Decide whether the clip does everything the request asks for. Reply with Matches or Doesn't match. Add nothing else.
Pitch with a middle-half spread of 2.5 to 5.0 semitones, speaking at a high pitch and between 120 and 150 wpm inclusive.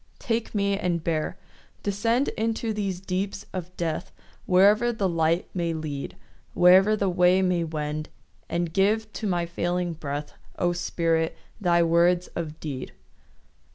Doesn't match